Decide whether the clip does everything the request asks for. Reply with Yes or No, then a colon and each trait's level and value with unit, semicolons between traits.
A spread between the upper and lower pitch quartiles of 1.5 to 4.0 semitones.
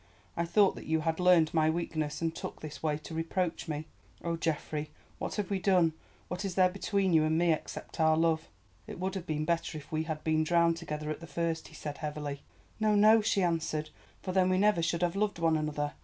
Yes: average, 2.7 semitones